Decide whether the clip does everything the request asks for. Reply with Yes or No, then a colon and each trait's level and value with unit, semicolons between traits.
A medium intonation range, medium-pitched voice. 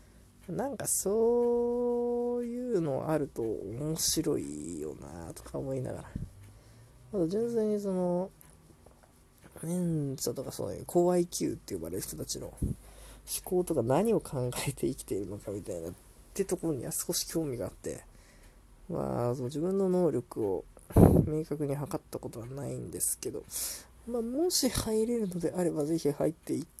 No: wide, 8.1 semitones; medium, 170 Hz